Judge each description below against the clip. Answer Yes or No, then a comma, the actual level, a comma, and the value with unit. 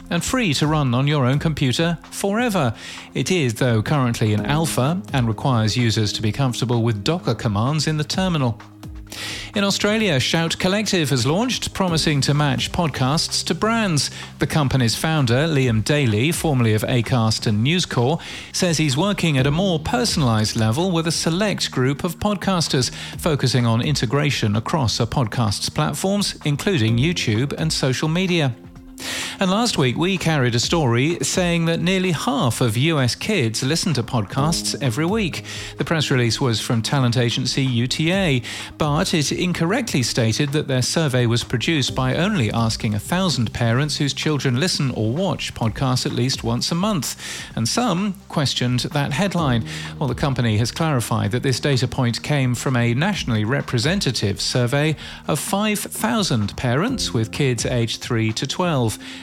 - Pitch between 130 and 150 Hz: Yes, low, 135 Hz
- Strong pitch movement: Yes, wide, 5.8 semitones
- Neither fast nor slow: Yes, average, 160 wpm